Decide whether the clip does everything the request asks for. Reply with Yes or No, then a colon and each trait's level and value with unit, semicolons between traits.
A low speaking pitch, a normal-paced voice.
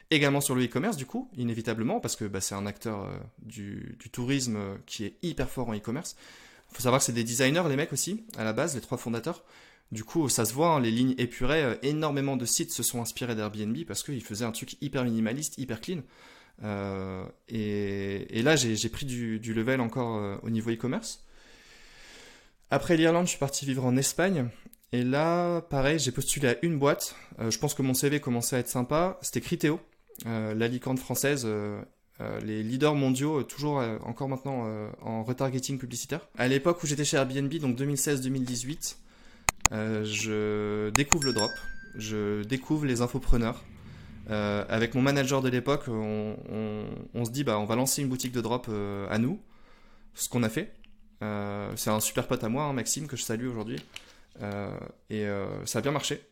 Yes: low, 125 Hz; average, 200 wpm